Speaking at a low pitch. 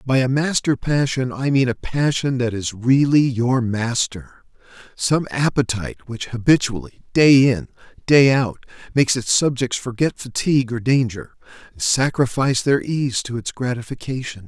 Yes: low, 125 Hz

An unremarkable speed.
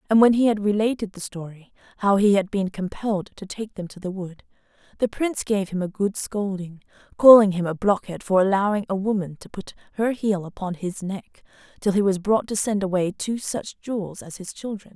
No: fast, 215 wpm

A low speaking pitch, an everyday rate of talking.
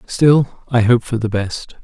Yes: low, 120 Hz; average, 195 wpm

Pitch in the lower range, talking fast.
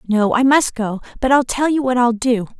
No: high, 245 Hz; fast, 255 wpm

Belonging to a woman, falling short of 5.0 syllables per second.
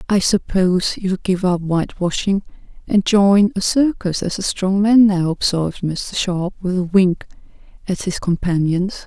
Yes: female; 4.5 syllables/s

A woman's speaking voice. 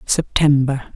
Yes: female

